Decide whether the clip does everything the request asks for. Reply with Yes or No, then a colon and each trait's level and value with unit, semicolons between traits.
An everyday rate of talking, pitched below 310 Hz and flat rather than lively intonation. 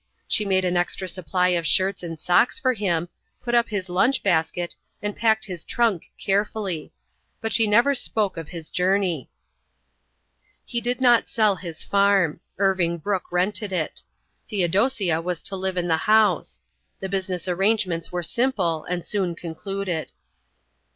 No: average, 150 wpm; high, 190 Hz; average, 3.3 semitones